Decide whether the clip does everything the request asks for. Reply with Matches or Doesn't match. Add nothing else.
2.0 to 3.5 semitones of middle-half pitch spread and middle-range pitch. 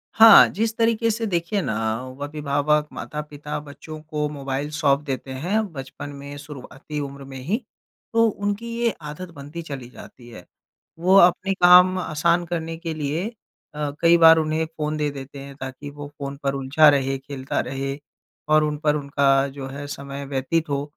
Matches